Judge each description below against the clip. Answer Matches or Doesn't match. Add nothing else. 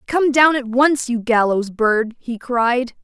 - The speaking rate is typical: Matches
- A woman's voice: Matches